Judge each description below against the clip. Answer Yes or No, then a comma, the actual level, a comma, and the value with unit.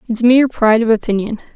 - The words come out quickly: No, average, 195 wpm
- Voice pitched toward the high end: Yes, high, 230 Hz